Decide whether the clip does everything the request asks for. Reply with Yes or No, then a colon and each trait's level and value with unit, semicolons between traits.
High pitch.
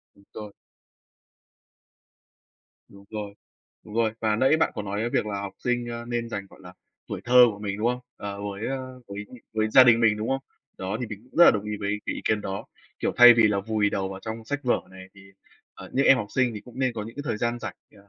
No: low, 110 Hz